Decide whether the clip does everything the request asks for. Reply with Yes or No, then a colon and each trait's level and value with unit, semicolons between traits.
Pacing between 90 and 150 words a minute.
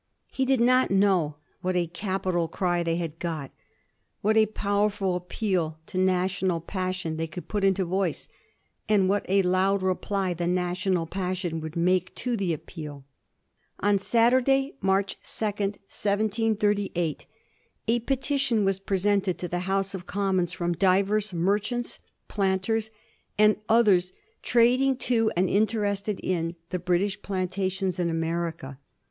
Yes: slow, 135 wpm